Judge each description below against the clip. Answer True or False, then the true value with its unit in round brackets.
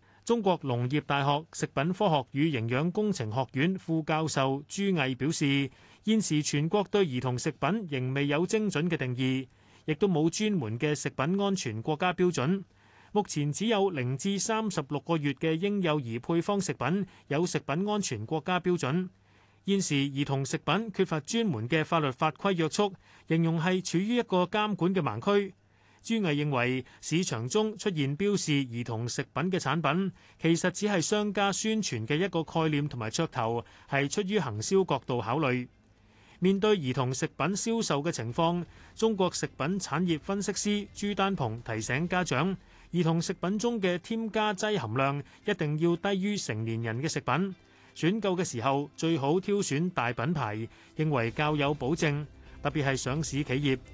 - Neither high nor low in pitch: True (160 Hz)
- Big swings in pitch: True (6.0 semitones)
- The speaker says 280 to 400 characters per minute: False (255 characters per minute)